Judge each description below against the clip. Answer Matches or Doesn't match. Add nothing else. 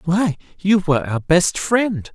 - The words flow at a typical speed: Matches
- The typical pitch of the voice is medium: Matches